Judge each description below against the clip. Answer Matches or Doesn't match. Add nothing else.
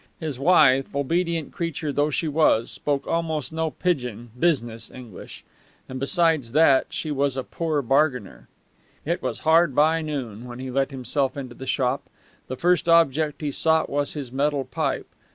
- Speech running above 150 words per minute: Matches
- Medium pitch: Matches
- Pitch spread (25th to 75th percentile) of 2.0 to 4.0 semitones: Matches